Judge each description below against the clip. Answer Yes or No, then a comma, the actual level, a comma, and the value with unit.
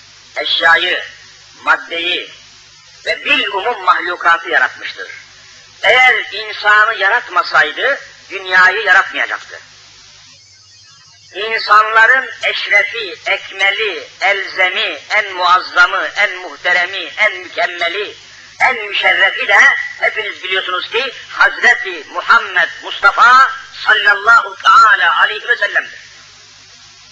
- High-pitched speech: Yes, high, 200 Hz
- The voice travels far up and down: Yes, wide, 6.5 semitones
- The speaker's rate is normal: No, slow, 75 wpm